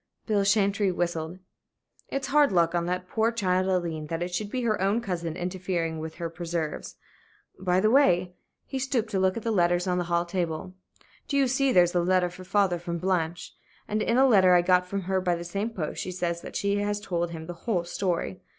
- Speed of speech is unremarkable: No, fast, 220 wpm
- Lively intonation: No, average, 2.9 semitones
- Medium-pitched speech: Yes, medium, 180 Hz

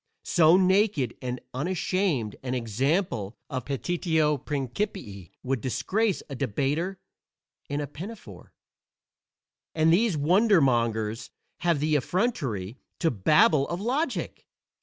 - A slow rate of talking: Yes, slow, 110 wpm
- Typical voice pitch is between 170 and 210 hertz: No, medium, 150 Hz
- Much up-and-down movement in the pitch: Yes, wide, 6.7 semitones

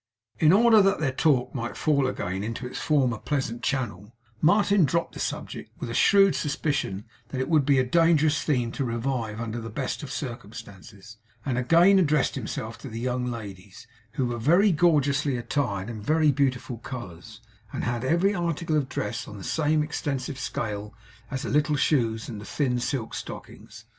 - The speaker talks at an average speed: Yes, average, 180 wpm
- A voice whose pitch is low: Yes, low, 130 Hz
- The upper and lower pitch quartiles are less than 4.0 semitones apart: No, average, 4.8 semitones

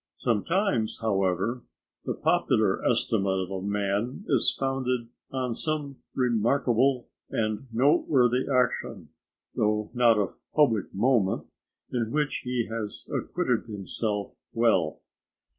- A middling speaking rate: No, slow, 110 wpm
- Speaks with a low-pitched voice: Yes, low, 115 Hz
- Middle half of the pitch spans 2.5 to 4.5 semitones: Yes, average, 3.8 semitones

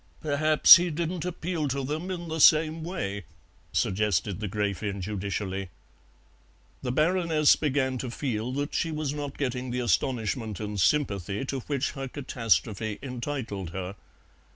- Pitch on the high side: No, low, 130 Hz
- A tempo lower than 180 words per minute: Yes, average, 140 wpm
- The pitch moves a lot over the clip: Yes, wide, 6.5 semitones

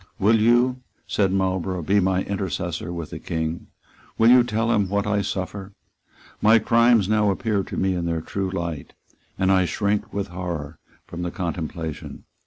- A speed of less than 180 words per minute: Yes, average, 170 wpm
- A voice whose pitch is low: Yes, very low, 95 Hz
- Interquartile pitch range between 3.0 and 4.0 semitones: Yes, average, 3.3 semitones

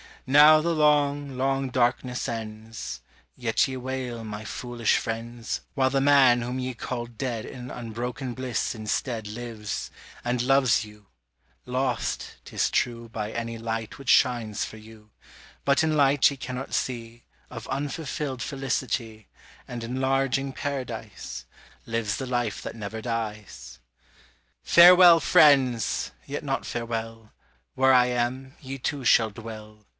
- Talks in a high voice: No, low, 120 Hz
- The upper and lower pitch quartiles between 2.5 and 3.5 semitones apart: Yes, average, 3.0 semitones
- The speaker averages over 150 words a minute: No, slow, 135 wpm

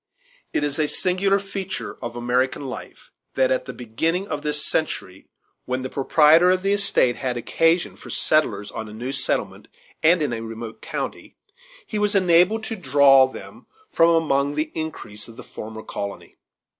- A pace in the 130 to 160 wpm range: No, average, 170 wpm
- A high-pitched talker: No, medium, 150 Hz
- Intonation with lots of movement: Yes, wide, 6.5 semitones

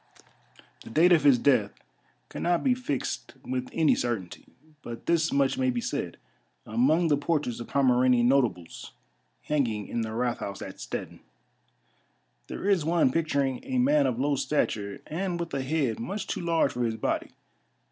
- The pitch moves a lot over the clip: Yes, wide, 5.8 semitones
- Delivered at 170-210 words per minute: No, average, 160 wpm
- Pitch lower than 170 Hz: Yes, medium, 140 Hz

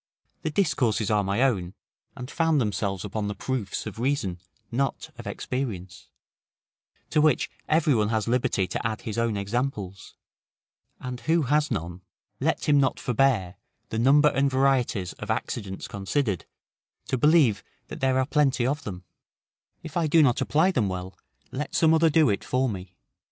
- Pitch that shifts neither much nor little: No, wide, 6.0 semitones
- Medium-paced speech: Yes, average, 165 wpm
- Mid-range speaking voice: No, low, 125 Hz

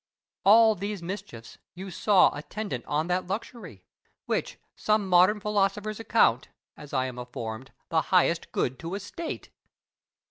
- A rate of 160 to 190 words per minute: No, average, 140 wpm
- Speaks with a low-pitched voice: No, medium, 185 Hz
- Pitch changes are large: Yes, wide, 6.2 semitones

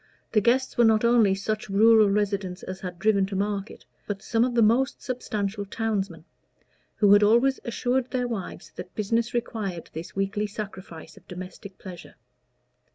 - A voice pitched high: Yes, high, 205 Hz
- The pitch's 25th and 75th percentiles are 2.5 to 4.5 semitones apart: Yes, average, 3.0 semitones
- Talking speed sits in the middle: Yes, average, 160 wpm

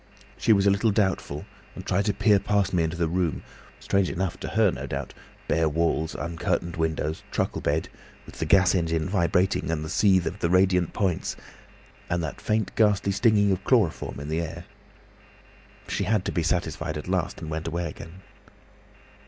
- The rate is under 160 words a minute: No, average, 180 wpm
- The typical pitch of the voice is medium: No, very low, 90 Hz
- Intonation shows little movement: No, average, 3.3 semitones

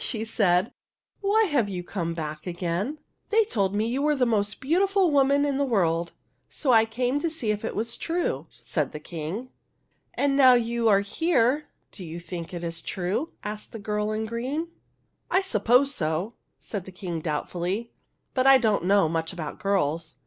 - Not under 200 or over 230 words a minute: Yes, fast, 205 wpm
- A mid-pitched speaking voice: No, high, 215 Hz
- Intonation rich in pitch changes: Yes, wide, 7.2 semitones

